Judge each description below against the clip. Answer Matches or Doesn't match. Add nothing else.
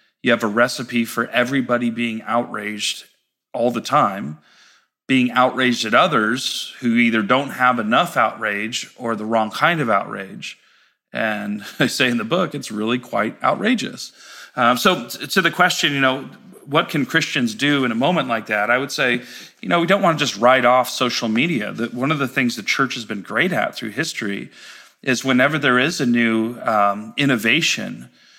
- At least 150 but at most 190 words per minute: Matches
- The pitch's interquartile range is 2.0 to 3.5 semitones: Matches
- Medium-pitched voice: Doesn't match